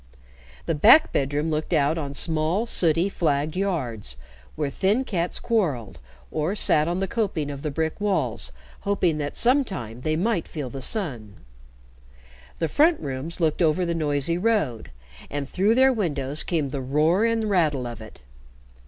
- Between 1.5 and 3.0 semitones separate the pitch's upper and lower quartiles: No, wide, 5.5 semitones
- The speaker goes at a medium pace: Yes, average, 160 wpm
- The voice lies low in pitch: No, medium, 160 Hz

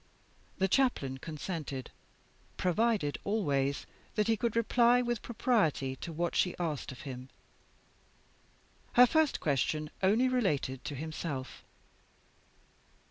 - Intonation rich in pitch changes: Yes, wide, 8.4 semitones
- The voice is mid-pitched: Yes, medium, 175 Hz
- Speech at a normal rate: No, slow, 110 wpm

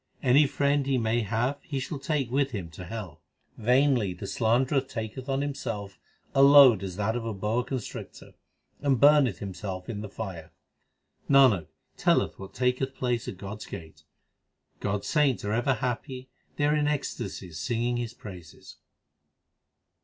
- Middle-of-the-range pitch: No, low, 120 Hz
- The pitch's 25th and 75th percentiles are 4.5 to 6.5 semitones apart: Yes, average, 5.0 semitones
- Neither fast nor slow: Yes, average, 165 wpm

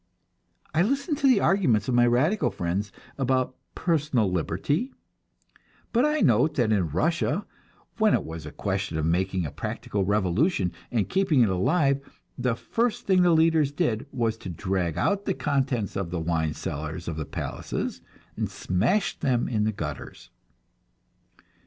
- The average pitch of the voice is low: Yes, low, 120 Hz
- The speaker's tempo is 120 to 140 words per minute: No, average, 160 wpm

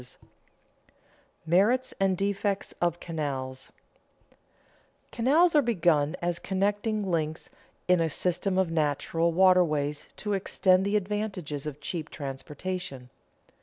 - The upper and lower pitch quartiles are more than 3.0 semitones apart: Yes, average, 4.6 semitones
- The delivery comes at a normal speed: No, slow, 110 wpm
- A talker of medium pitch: Yes, medium, 180 Hz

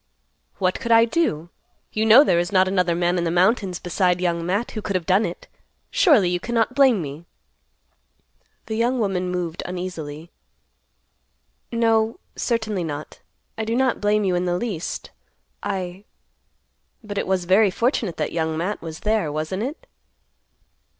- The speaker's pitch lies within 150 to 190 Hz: Yes, medium, 185 Hz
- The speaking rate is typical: Yes, average, 155 wpm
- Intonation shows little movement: No, average, 4.2 semitones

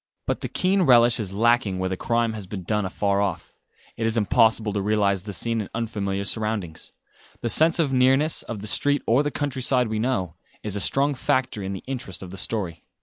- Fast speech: Yes, fast, 210 wpm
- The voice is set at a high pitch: No, low, 110 Hz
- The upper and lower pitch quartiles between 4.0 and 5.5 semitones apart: Yes, average, 4.4 semitones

